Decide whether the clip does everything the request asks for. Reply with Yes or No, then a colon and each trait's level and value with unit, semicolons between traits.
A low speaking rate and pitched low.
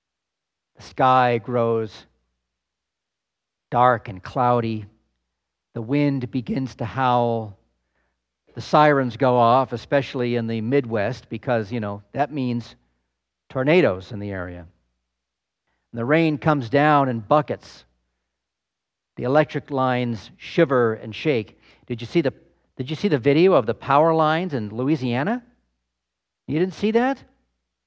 Yes: slow, 130 wpm; low, 120 Hz